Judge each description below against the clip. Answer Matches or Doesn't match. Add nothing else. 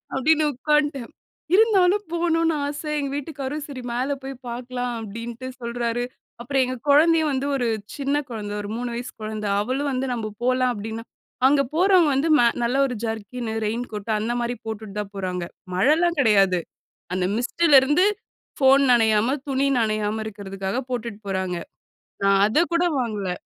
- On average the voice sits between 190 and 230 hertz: Doesn't match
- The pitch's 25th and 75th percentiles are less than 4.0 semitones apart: Doesn't match